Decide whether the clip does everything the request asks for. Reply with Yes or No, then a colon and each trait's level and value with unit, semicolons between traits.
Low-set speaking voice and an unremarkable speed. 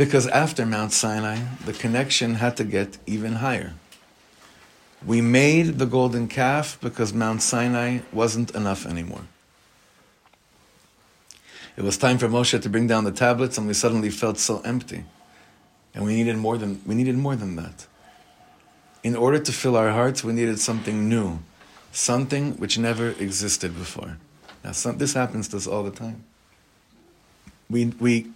Yes: low, 115 Hz; average, 155 wpm